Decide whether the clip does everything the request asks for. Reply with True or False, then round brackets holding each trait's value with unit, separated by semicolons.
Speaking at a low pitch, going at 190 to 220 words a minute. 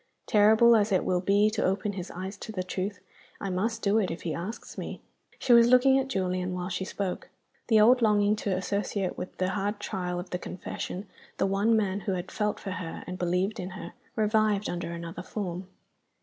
False (195 Hz; 205 wpm)